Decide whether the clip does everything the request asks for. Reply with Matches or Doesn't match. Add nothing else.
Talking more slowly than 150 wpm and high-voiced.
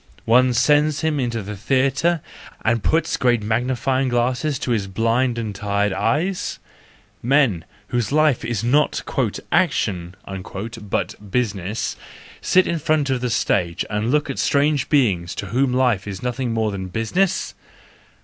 Doesn't match